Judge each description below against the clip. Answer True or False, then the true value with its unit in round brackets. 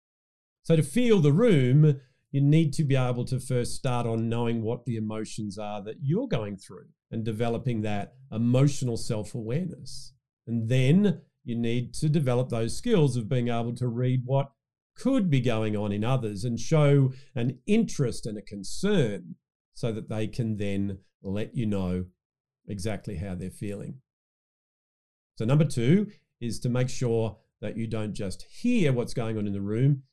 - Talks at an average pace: True (170 wpm)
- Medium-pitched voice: False (120 Hz)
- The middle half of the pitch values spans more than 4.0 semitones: True (4.4 semitones)